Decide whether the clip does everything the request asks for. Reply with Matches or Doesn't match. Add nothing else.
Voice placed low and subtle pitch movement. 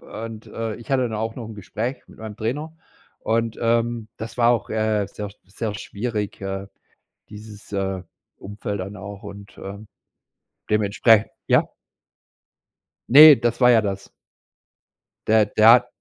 Matches